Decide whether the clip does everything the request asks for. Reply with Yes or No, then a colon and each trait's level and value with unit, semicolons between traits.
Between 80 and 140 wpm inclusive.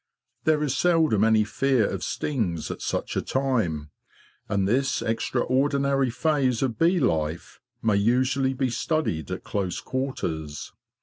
Yes: slow, 135 wpm